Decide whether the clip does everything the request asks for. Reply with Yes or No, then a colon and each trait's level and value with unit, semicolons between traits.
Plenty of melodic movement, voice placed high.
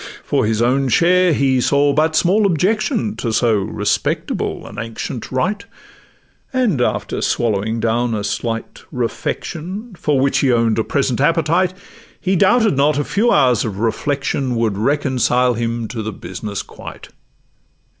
No: wide, 6.7 semitones; low, 130 Hz